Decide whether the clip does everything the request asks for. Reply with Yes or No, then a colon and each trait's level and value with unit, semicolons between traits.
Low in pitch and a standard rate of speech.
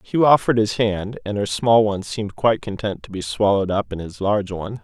No: low, 105 Hz; fast, 235 wpm